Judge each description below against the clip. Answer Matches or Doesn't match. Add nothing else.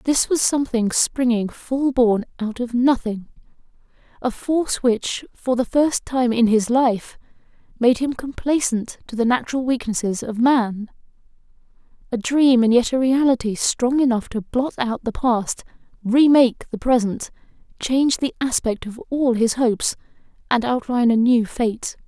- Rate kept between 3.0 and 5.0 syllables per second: Matches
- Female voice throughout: Matches